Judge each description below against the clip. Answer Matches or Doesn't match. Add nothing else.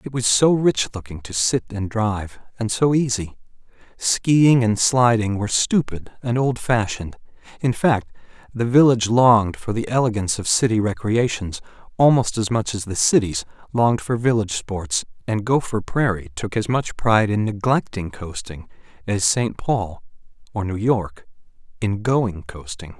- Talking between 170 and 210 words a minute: Doesn't match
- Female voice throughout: Doesn't match